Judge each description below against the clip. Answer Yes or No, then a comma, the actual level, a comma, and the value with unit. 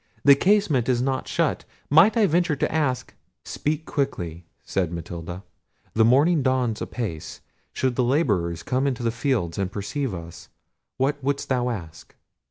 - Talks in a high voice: No, low, 125 Hz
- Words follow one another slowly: No, average, 150 wpm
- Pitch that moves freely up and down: Yes, wide, 7.1 semitones